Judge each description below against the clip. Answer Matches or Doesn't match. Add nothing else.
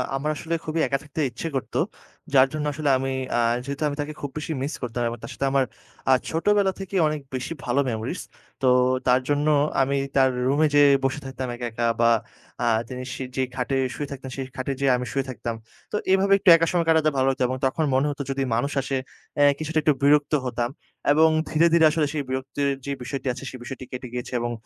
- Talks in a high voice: Doesn't match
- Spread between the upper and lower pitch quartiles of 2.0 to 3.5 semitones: Matches